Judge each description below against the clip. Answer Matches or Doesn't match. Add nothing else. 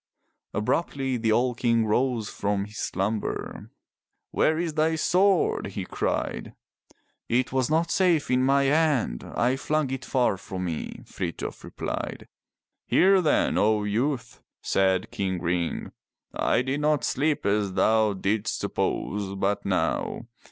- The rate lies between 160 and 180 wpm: Doesn't match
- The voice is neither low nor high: Doesn't match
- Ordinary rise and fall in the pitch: Doesn't match